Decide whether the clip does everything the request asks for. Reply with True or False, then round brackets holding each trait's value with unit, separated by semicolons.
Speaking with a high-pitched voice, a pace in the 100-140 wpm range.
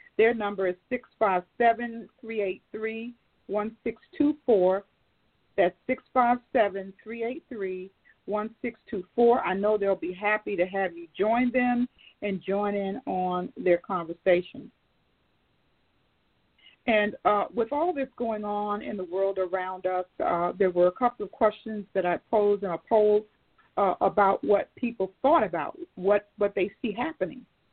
True (205 Hz; 135 wpm)